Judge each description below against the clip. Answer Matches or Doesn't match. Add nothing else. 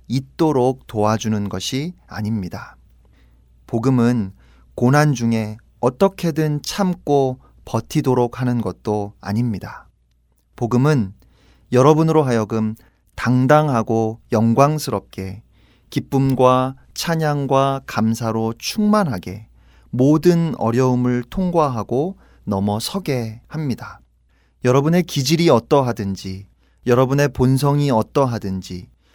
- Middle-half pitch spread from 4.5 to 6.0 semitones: Matches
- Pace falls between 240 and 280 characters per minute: Doesn't match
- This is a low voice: Matches